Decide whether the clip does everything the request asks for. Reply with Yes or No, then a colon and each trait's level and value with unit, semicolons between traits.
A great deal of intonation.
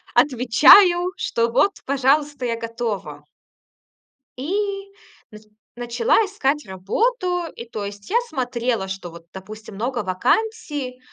Yes: wide, 8.5 semitones